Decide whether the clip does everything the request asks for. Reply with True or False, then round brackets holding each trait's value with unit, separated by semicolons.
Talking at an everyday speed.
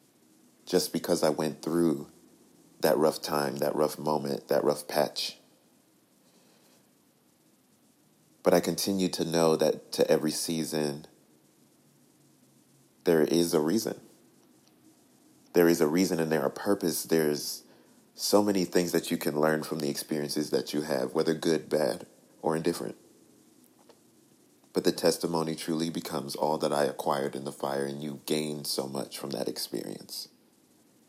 True (145 wpm)